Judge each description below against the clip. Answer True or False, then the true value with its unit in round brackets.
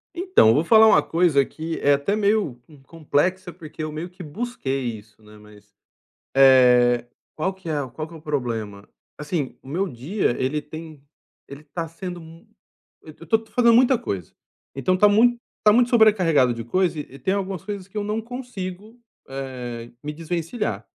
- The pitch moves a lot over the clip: True (6.8 semitones)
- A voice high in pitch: False (165 Hz)